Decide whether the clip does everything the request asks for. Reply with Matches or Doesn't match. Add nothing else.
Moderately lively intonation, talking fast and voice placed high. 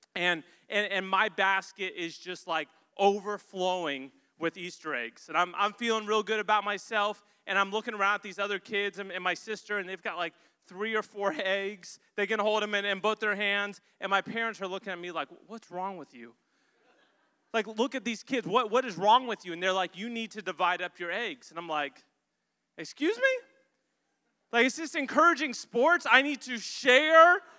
Matches